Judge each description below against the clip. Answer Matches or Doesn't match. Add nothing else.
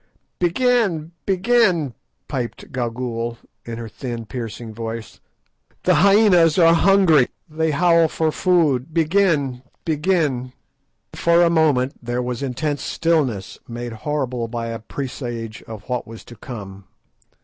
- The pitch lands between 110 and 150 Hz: Matches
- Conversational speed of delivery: Doesn't match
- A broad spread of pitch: Matches